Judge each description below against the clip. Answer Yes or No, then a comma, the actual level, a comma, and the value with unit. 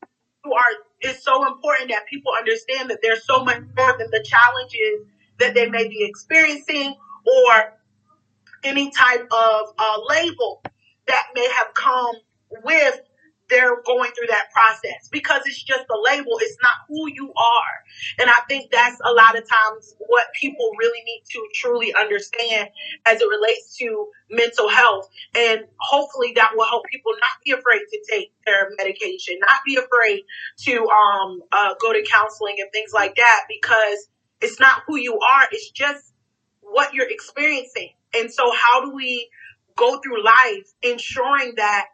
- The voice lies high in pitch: Yes, very high, 255 Hz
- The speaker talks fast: No, average, 165 wpm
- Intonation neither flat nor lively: No, wide, 6.0 semitones